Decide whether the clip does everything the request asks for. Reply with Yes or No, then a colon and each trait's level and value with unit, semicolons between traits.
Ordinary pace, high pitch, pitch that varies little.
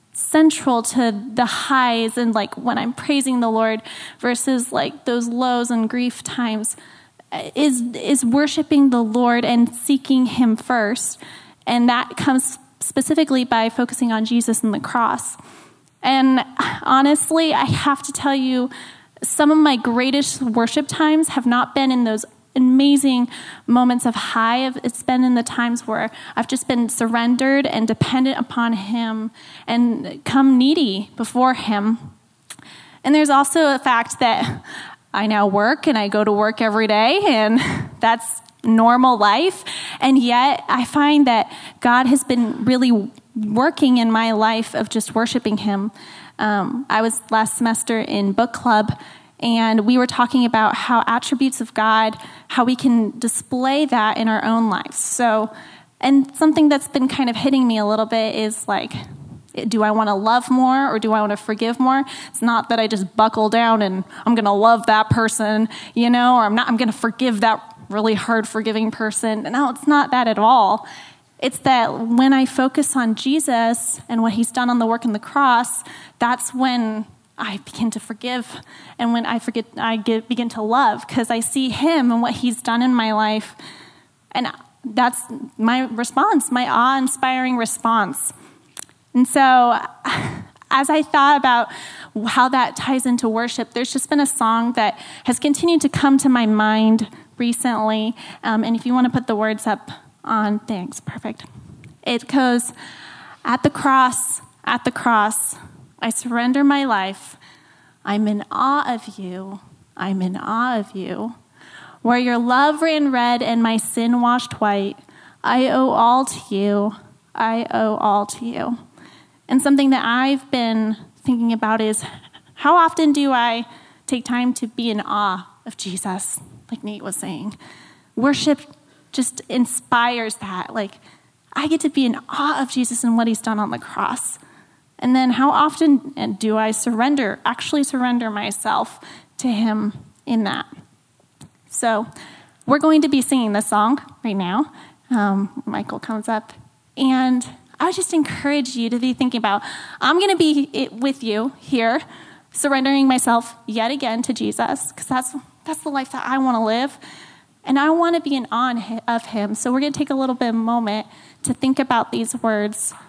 No: average, 170 wpm; high, 240 Hz; average, 3.0 semitones